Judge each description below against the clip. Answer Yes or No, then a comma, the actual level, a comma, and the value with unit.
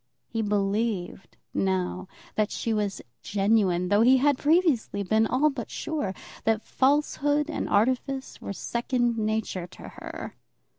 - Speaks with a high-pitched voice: Yes, high, 220 Hz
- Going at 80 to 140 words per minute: Yes, slow, 135 wpm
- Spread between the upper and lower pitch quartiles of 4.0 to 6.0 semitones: Yes, average, 4.7 semitones